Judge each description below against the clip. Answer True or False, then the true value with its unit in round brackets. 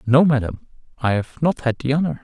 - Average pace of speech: False (215 wpm)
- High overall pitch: False (135 Hz)